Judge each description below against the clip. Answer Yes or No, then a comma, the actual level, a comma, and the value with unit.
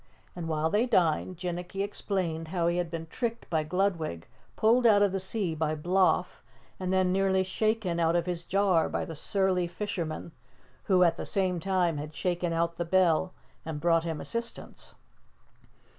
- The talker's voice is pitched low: No, medium, 180 Hz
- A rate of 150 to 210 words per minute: Yes, average, 175 wpm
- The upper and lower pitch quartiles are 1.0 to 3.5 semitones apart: Yes, average, 2.7 semitones